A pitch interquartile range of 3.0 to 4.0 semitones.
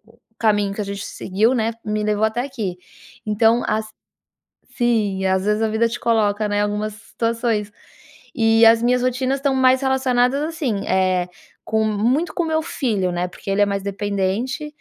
Yes: average, 3.3 semitones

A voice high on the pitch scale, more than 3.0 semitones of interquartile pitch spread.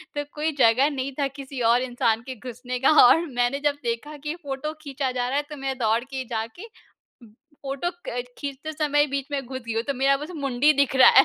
No: very high, 270 Hz; average, 2.7 semitones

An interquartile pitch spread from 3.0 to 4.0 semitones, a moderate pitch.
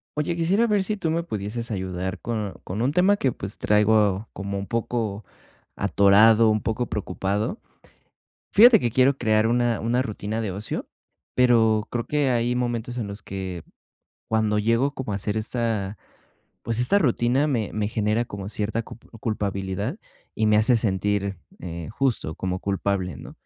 No: average, 3.4 semitones; low, 110 Hz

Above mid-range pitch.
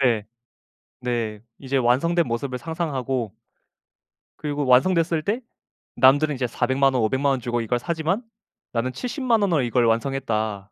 No: low, 130 Hz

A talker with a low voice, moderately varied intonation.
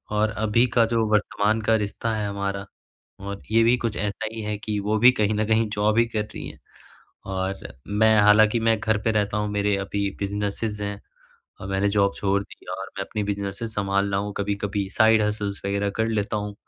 No: low, 105 Hz; narrow, 1.6 semitones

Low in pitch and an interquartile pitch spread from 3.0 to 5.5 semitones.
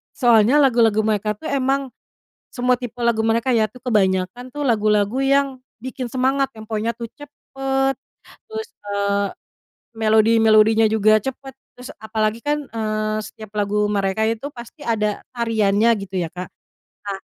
No: high, 225 Hz; average, 3.4 semitones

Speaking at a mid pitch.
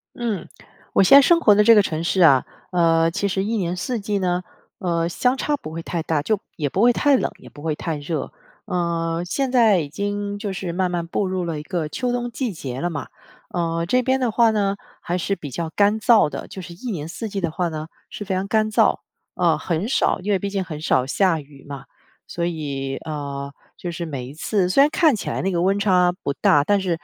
Yes: medium, 180 Hz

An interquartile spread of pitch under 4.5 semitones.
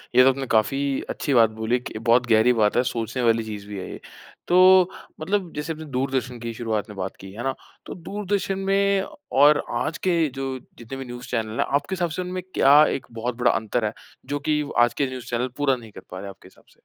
No: average, 4.8 semitones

